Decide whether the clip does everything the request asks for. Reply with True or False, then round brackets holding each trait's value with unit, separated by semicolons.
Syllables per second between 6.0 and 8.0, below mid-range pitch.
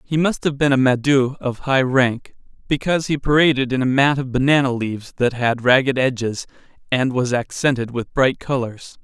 False (5.1 syllables/s; 130 Hz)